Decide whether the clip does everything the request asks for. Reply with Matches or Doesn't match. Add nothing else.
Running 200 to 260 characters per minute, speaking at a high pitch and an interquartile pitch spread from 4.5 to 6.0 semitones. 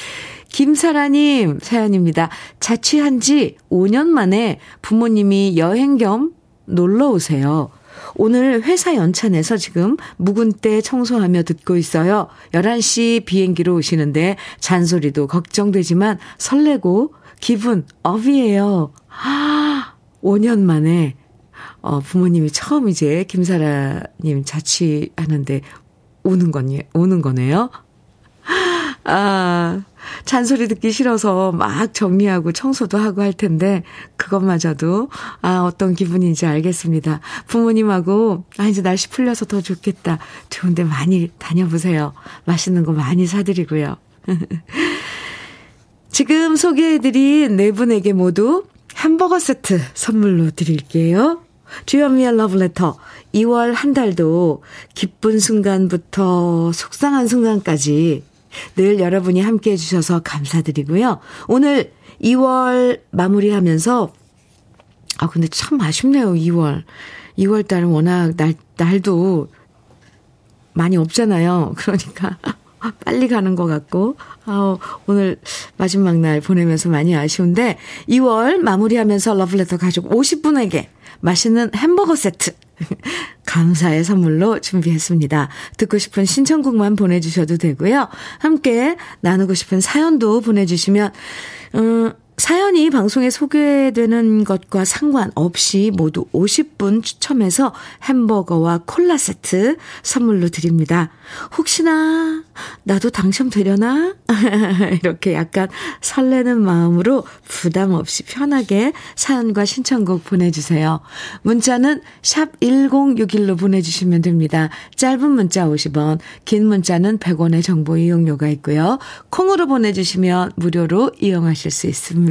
Matches